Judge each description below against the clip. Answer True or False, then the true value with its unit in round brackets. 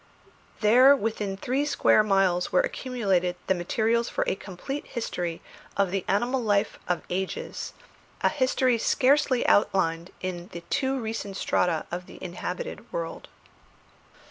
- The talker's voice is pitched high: True (205 Hz)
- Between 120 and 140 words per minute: True (135 wpm)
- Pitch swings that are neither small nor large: False (5.8 semitones)